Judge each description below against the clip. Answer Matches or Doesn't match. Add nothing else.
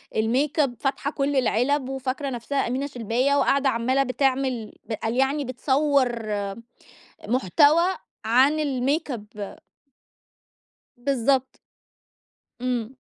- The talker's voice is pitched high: Matches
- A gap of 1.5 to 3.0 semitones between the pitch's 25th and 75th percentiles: Matches